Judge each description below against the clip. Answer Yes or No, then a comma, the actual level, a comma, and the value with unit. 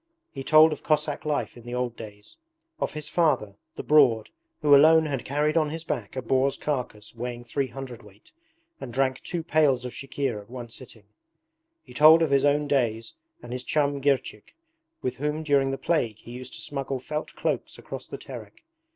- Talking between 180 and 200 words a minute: Yes, average, 190 wpm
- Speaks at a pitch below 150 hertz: Yes, low, 135 Hz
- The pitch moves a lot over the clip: No, average, 3.7 semitones